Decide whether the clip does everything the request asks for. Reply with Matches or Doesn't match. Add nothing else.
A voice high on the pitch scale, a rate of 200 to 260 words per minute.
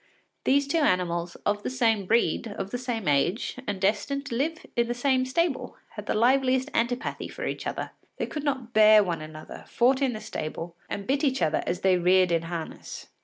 Matches